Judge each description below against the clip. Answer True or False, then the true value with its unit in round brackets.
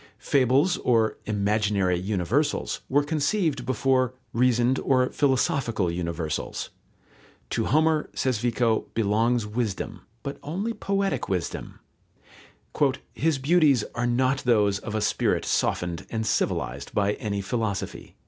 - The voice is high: False (120 Hz)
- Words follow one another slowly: True (115 wpm)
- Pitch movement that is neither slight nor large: True (5.0 semitones)